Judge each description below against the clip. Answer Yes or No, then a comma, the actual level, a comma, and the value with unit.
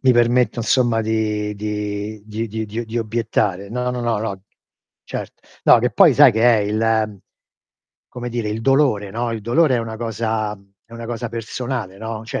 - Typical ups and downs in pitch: No, narrow, 1.9 semitones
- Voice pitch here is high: No, low, 110 Hz